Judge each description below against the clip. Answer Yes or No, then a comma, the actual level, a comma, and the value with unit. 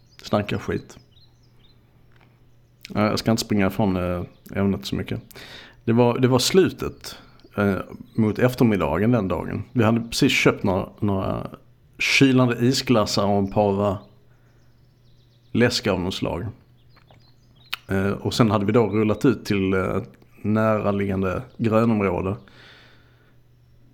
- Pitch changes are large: No, average, 3.2 semitones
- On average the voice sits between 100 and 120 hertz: Yes, low, 115 Hz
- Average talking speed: No, slow, 120 wpm